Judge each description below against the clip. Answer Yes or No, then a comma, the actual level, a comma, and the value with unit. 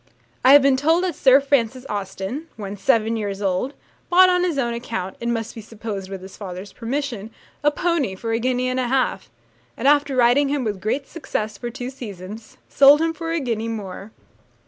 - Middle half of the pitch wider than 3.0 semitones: Yes, average, 5.1 semitones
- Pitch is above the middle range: Yes, high, 240 Hz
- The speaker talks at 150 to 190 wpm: No, average, 200 wpm